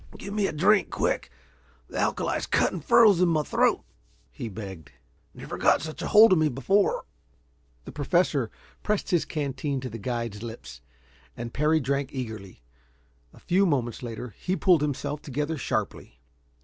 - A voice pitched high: No, medium, 140 Hz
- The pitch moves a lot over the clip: Yes, wide, 6.7 semitones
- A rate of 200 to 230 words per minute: No, average, 160 wpm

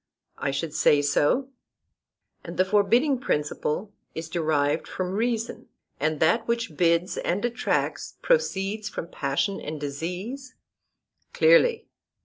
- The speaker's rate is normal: No, slow, 120 wpm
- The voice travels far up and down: Yes, wide, 7.2 semitones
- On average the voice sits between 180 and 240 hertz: Yes, medium, 185 Hz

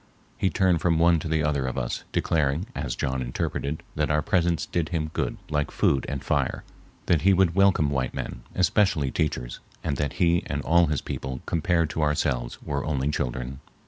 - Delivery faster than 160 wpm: Yes, average, 190 wpm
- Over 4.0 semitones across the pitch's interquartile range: No, average, 3.7 semitones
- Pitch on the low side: Yes, very low, 75 Hz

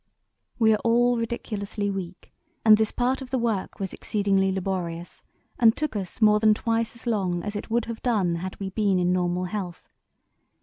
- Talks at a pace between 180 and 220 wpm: Yes, average, 185 wpm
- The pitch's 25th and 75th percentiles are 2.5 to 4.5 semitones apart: Yes, average, 3.5 semitones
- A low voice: No, high, 210 Hz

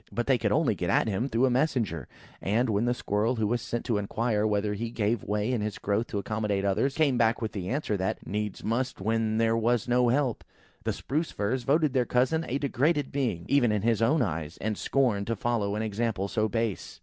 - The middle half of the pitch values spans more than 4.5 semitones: No, average, 3.2 semitones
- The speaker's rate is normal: No, fast, 230 wpm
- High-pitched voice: No, low, 115 Hz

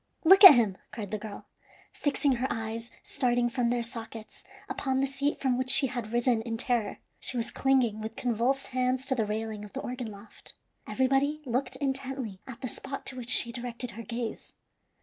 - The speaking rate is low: No, average, 190 wpm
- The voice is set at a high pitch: Yes, high, 245 Hz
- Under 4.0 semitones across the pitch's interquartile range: Yes, average, 2.8 semitones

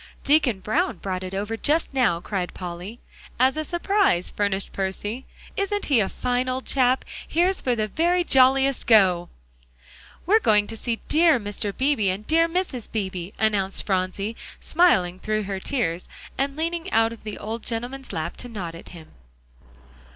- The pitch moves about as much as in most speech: No, wide, 6.1 semitones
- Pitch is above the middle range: Yes, high, 225 Hz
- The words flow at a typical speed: Yes, average, 165 wpm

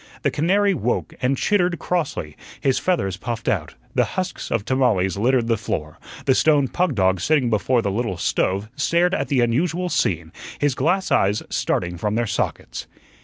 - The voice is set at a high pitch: No, low, 125 Hz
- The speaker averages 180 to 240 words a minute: No, average, 170 wpm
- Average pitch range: No, wide, 8.1 semitones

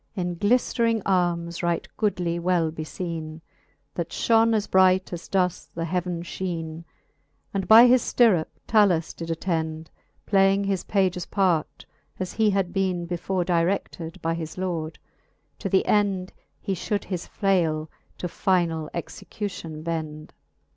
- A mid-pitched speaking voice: Yes, medium, 180 Hz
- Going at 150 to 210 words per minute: No, slow, 135 wpm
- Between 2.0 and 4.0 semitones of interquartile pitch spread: Yes, average, 2.8 semitones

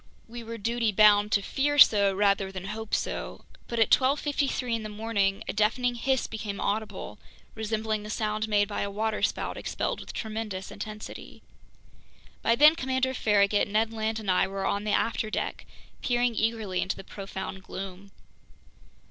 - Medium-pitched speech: No, high, 215 Hz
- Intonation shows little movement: Yes, narrow, 2.2 semitones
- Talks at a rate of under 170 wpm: Yes, average, 160 wpm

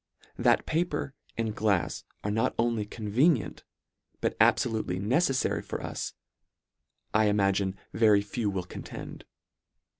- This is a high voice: No, low, 110 Hz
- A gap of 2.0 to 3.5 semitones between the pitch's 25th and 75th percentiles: Yes, average, 2.9 semitones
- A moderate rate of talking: No, slow, 120 wpm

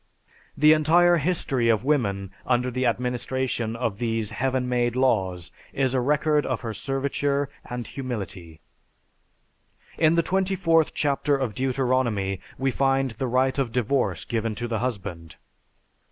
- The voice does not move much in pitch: No, average, 3.5 semitones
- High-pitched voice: No, low, 125 Hz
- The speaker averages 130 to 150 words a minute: Yes, average, 140 wpm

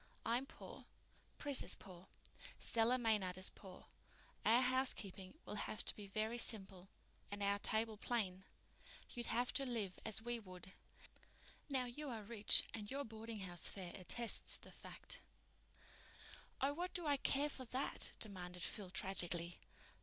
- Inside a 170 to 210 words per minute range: No, average, 140 wpm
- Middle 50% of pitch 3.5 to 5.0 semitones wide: Yes, average, 4.4 semitones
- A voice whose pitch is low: No, high, 220 Hz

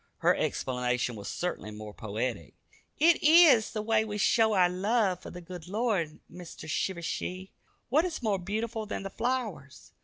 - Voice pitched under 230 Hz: Yes, high, 190 Hz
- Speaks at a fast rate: No, average, 160 wpm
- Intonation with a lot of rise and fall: Yes, wide, 6.3 semitones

